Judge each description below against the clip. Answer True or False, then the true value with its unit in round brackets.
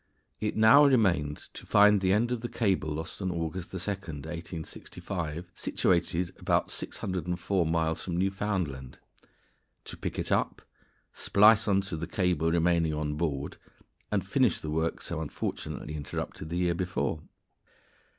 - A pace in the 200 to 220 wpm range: False (145 wpm)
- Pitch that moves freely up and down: False (3.4 semitones)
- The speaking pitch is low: True (85 Hz)